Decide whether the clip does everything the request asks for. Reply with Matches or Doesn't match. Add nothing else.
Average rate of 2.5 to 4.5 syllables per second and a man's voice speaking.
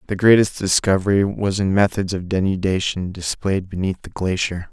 Doesn't match